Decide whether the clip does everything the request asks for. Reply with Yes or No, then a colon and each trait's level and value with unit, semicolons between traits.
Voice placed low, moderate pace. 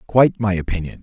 Yes: low, 100 Hz; average, 175 wpm